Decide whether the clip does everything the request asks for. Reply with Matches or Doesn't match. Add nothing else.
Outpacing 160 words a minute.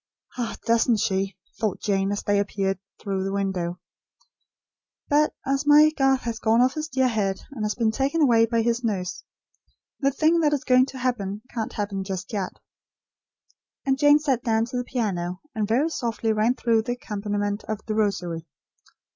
Matches